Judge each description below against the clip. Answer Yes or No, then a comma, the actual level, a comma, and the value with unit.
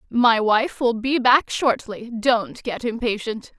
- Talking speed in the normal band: Yes, average, 150 wpm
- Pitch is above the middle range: Yes, high, 235 Hz